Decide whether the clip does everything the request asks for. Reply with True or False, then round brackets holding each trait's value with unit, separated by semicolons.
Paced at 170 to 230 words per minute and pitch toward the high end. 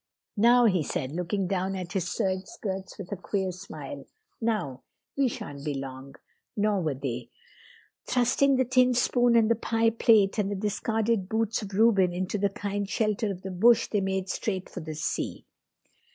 True (180 wpm; 195 Hz)